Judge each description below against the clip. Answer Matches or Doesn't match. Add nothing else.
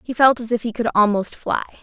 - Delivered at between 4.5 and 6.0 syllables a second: Matches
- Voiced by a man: Doesn't match